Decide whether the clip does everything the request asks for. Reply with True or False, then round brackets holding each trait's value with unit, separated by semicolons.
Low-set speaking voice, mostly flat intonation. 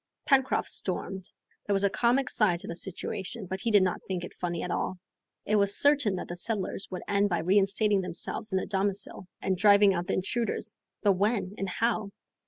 False (195 Hz; 2.3 semitones)